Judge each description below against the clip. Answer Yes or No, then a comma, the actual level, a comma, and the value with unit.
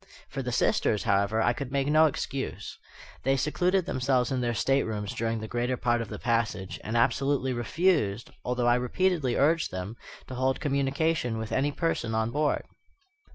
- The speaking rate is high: No, average, 170 wpm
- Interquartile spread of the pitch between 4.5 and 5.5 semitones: No, average, 3.5 semitones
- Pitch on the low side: Yes, low, 125 Hz